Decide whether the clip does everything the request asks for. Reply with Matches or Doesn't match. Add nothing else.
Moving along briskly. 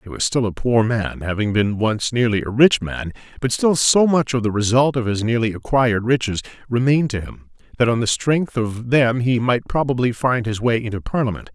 Matches